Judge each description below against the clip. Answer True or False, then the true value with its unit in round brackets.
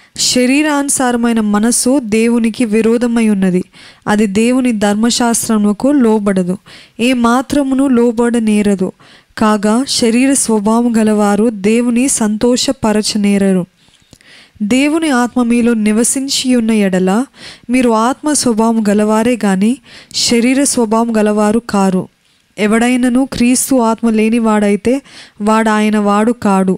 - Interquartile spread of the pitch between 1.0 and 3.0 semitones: True (2.6 semitones)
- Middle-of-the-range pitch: False (230 Hz)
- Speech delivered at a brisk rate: False (95 wpm)